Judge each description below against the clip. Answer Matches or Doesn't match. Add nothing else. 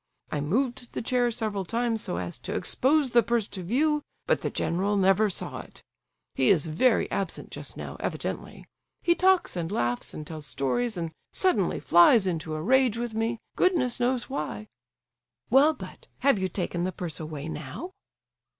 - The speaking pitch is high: Matches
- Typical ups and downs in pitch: Doesn't match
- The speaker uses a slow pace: Doesn't match